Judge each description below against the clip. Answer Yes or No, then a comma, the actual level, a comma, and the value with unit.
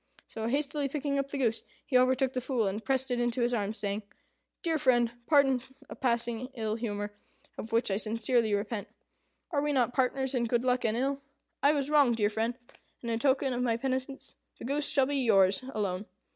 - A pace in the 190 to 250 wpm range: Yes, average, 200 wpm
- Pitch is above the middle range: Yes, high, 245 Hz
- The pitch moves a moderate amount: Yes, average, 3.2 semitones